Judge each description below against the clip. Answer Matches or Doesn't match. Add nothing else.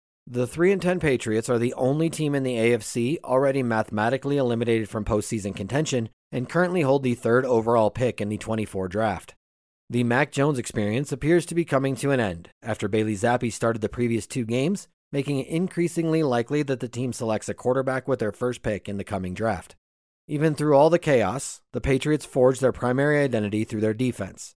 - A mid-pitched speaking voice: Doesn't match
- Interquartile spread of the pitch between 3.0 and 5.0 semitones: Matches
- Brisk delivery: Doesn't match